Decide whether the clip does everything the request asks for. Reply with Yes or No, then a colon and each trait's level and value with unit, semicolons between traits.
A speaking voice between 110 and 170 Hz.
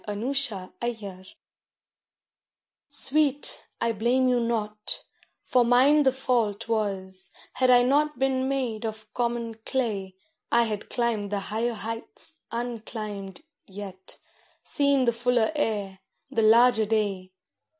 No: high, 230 Hz